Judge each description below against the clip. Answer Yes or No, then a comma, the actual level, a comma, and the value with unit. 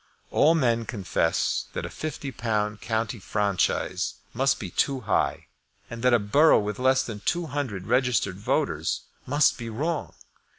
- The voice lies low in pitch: Yes, low, 115 Hz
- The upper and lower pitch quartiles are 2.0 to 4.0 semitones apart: No, average, 4.5 semitones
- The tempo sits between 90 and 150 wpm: Yes, average, 145 wpm